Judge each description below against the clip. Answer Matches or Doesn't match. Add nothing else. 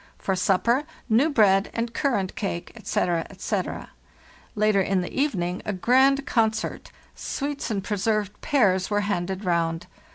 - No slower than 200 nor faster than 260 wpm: Doesn't match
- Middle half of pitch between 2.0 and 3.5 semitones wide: Doesn't match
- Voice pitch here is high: Matches